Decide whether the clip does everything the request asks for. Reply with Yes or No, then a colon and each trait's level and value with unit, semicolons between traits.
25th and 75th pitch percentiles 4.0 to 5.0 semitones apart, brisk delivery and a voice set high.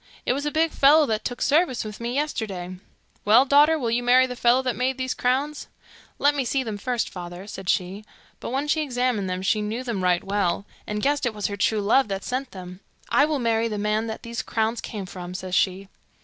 Yes: average, 4.6 semitones; fast, 230 wpm; high, 230 Hz